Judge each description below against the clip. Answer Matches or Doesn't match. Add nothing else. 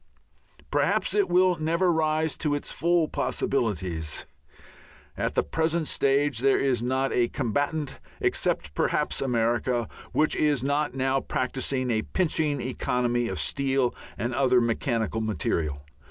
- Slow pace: Matches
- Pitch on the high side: Doesn't match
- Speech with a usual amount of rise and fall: Matches